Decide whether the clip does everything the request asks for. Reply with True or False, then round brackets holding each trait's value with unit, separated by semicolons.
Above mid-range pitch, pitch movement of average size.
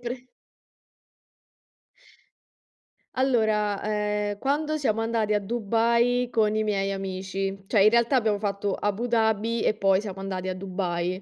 True (210 Hz; 3.0 semitones)